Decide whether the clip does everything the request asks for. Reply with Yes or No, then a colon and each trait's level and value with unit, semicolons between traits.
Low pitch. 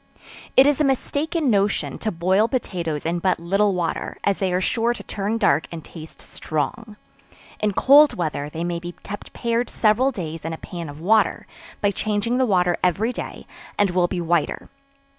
No: high, 195 Hz